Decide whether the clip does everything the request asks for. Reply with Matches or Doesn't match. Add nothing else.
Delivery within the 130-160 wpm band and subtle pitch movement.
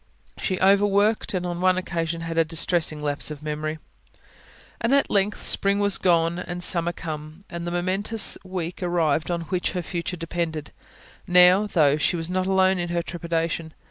Doesn't match